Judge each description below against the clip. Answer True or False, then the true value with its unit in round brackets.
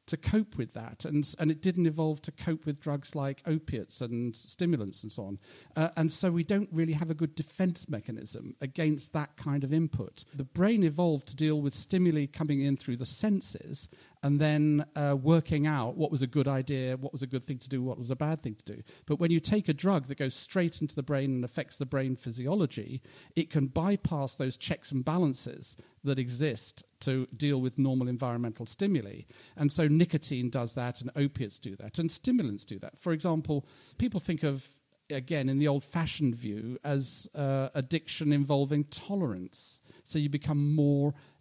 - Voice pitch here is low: False (145 Hz)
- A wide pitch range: False (3.5 semitones)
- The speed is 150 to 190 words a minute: False (200 wpm)